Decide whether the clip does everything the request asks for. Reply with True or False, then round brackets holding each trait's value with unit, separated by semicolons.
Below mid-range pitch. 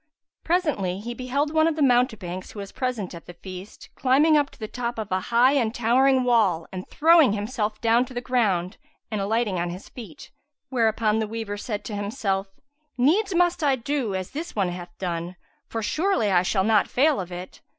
False (225 Hz)